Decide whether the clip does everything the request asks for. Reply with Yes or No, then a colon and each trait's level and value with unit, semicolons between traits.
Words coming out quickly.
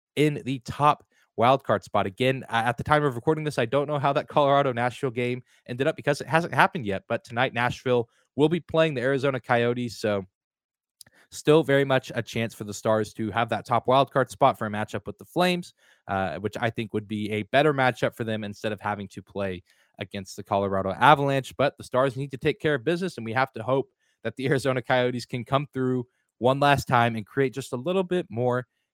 Yes: fast, 225 wpm